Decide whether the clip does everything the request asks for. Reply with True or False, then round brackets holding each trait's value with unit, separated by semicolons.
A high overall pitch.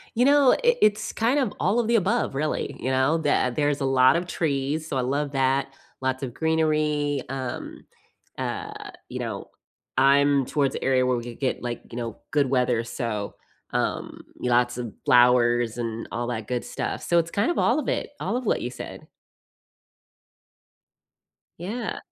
False (135 Hz)